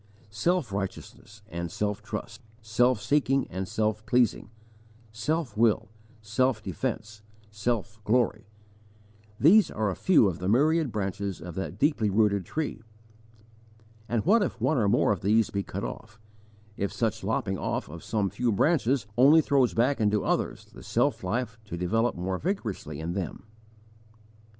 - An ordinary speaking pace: Yes, average, 150 wpm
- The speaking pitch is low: Yes, low, 110 Hz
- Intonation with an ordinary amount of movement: Yes, average, 4.2 semitones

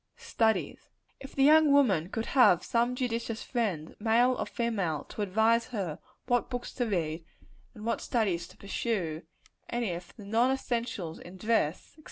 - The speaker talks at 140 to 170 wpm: Yes, average, 165 wpm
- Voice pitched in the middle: No, high, 225 Hz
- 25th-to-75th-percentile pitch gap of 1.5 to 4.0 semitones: No, average, 5.0 semitones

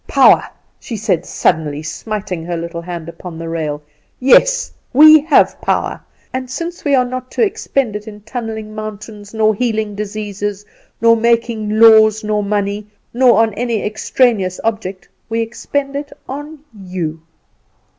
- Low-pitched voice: No, high, 215 Hz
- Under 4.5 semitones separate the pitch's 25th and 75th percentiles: Yes, average, 3.7 semitones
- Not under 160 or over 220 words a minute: No, average, 145 wpm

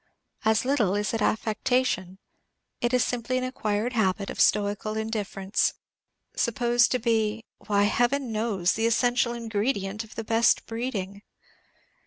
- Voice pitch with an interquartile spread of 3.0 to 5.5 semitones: No, narrow, 2.6 semitones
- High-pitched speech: Yes, high, 225 Hz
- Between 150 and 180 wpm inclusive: No, slow, 135 wpm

